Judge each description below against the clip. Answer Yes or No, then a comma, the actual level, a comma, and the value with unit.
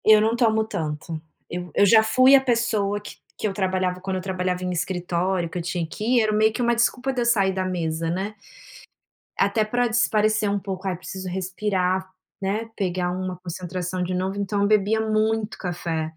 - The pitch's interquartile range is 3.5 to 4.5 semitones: No, average, 3.1 semitones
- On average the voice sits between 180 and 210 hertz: Yes, high, 190 Hz